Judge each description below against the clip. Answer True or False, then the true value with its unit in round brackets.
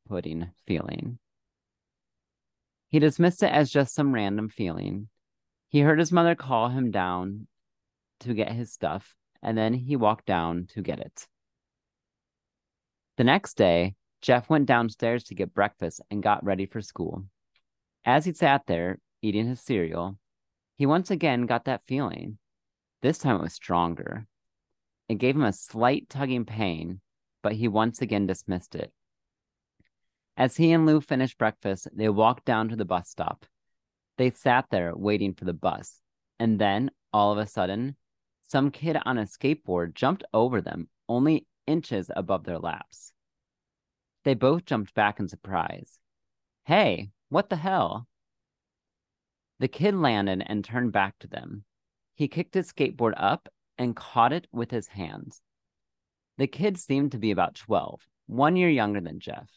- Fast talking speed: False (155 wpm)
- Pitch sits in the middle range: False (110 Hz)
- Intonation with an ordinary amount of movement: False (5.8 semitones)